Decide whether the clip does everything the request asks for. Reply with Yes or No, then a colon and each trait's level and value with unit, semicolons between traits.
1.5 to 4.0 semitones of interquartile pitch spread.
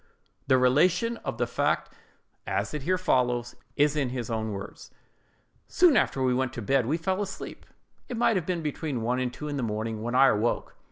No: wide, 5.5 semitones